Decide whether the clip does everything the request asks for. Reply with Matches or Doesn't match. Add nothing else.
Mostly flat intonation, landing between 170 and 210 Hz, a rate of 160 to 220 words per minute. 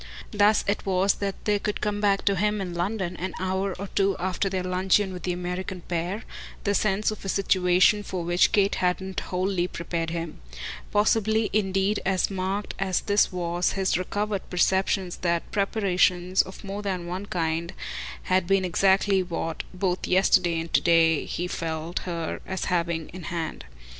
Matches